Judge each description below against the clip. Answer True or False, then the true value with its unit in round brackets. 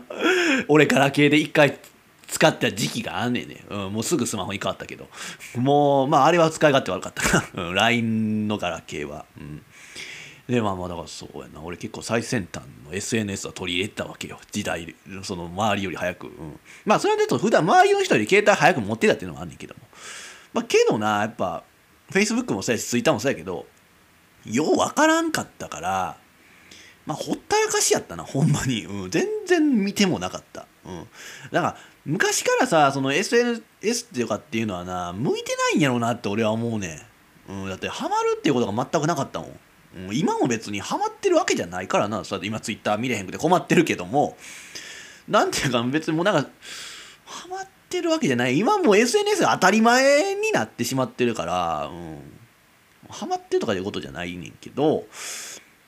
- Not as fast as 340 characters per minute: False (425 characters per minute)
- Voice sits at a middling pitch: False (130 Hz)